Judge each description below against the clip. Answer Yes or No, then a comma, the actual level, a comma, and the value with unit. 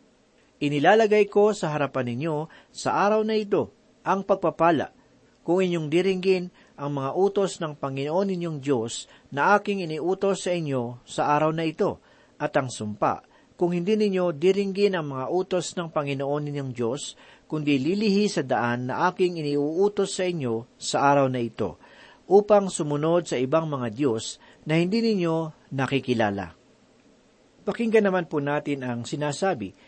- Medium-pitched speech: Yes, medium, 165 Hz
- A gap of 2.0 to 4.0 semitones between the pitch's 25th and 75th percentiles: No, average, 5.2 semitones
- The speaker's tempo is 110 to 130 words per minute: No, average, 145 wpm